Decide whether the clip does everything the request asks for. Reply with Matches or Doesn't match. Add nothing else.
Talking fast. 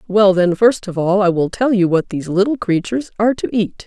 Matches